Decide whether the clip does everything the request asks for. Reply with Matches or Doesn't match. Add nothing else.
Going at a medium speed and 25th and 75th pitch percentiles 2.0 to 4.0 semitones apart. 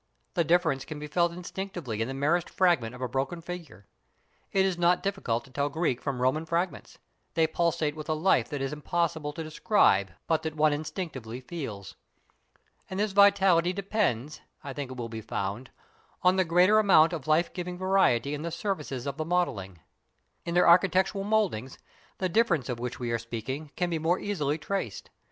Doesn't match